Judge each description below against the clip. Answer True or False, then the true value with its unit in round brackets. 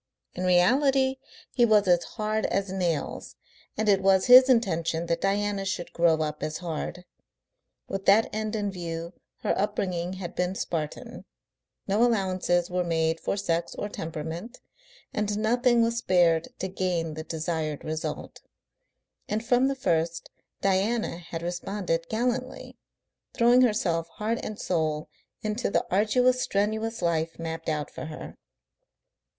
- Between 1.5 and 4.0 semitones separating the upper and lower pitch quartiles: False (4.6 semitones)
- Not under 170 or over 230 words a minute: False (140 wpm)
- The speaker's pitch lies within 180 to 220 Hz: True (190 Hz)